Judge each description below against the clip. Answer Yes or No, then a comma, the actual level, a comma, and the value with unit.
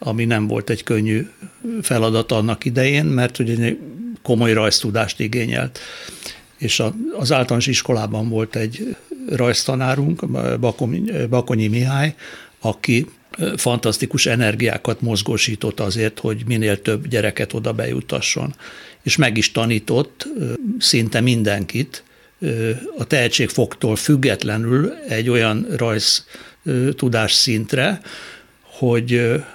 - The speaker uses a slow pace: Yes, slow, 100 wpm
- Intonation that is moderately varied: Yes, average, 3.0 semitones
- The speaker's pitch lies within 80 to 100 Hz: No, low, 115 Hz